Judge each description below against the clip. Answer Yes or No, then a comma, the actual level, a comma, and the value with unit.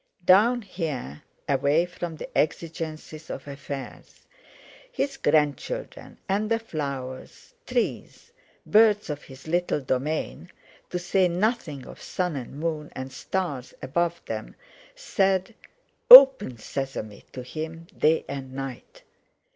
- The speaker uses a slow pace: Yes, slow, 110 wpm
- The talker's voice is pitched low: No, medium, 160 Hz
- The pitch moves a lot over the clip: Yes, wide, 5.7 semitones